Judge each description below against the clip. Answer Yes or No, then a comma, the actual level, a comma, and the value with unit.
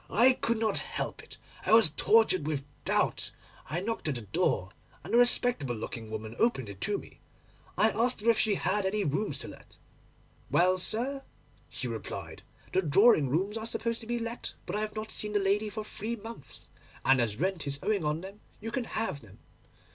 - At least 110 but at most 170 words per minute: No, average, 200 wpm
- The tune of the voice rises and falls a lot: Yes, wide, 7.5 semitones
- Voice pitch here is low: No, high, 205 Hz